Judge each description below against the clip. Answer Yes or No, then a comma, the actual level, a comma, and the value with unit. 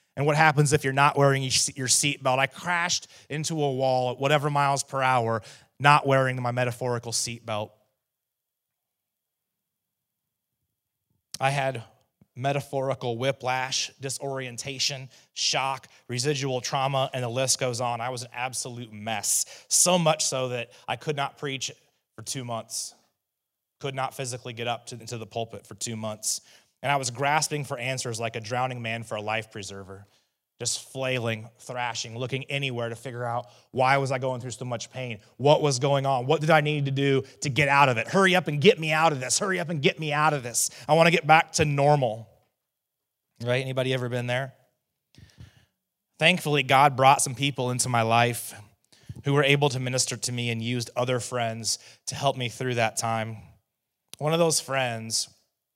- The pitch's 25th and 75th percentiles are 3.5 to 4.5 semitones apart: No, average, 3.0 semitones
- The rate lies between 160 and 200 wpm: Yes, average, 180 wpm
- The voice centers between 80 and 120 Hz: No, low, 130 Hz